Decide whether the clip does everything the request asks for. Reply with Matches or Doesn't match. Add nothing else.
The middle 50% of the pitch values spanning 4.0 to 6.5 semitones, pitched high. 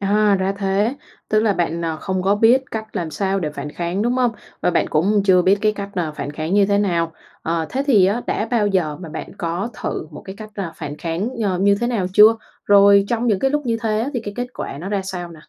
Doesn't match